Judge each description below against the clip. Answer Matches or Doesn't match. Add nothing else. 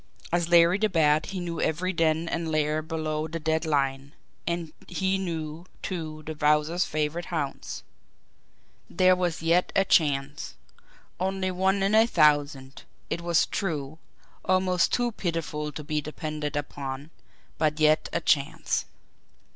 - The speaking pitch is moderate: Matches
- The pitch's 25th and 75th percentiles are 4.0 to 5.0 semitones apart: Doesn't match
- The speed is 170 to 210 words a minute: Doesn't match